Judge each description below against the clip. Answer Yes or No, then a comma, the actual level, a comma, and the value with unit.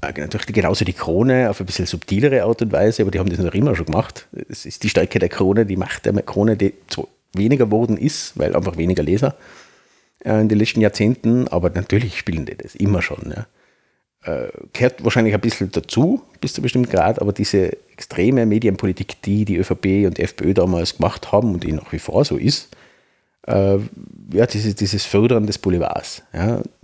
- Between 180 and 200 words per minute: Yes, fast, 190 wpm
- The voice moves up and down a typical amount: Yes, average, 3.3 semitones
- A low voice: Yes, low, 100 Hz